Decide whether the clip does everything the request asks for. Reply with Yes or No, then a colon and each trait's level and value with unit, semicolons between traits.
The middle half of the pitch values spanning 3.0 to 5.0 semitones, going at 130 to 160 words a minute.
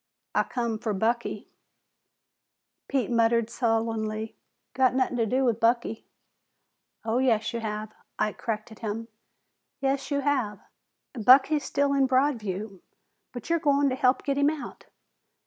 Yes: average, 3.4 semitones; slow, 135 wpm